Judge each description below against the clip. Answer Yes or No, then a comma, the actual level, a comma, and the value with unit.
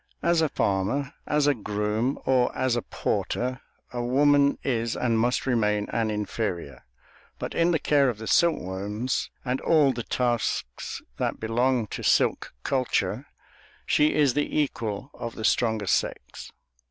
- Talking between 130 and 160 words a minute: Yes, average, 150 wpm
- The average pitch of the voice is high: No, low, 120 Hz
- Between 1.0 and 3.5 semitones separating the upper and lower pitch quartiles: No, average, 4.3 semitones